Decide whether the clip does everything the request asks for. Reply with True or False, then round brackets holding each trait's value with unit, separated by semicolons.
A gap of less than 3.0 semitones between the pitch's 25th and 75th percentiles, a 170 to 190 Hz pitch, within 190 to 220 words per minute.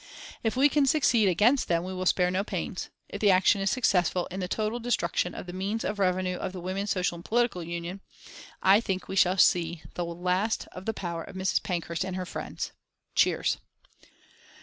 True (2.6 semitones; 185 Hz; 200 wpm)